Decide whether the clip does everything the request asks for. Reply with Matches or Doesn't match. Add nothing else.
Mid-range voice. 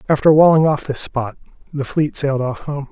Matches